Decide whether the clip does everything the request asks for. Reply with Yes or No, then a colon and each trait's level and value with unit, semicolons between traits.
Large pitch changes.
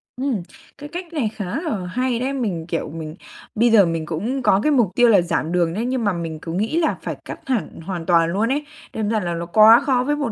Yes: wide, 6.9 semitones